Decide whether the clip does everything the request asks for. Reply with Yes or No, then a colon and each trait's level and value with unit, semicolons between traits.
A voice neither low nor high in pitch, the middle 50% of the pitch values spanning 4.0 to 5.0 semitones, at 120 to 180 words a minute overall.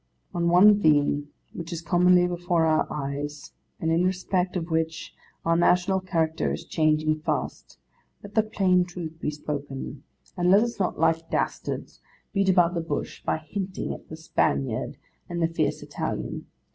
No: medium, 170 Hz; narrow, 2.6 semitones; average, 160 wpm